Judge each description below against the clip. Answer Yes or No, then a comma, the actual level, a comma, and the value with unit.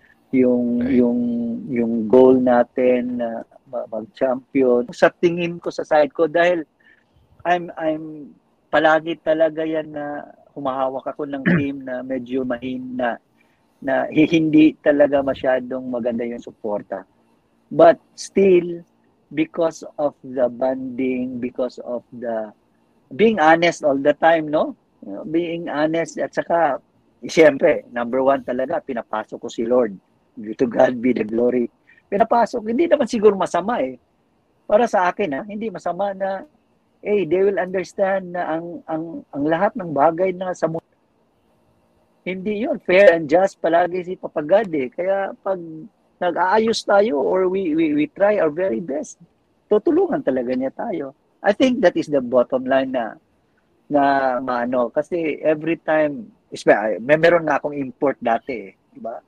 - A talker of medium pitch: Yes, medium, 155 Hz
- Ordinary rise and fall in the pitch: No, wide, 6.2 semitones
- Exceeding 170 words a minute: No, average, 145 wpm